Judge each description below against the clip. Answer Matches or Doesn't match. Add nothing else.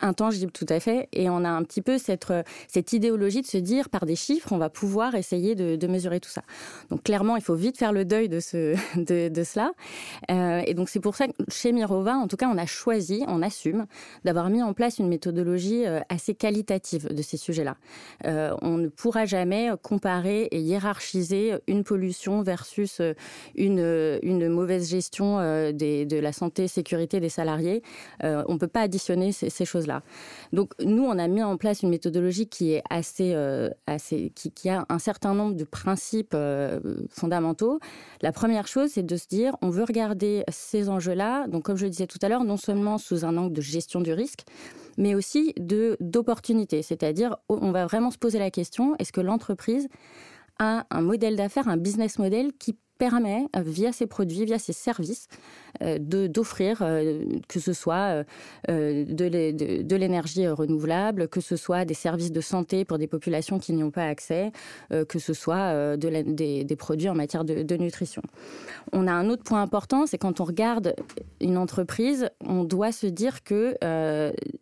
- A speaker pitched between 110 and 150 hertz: Doesn't match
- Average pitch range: Matches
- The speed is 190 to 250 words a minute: Matches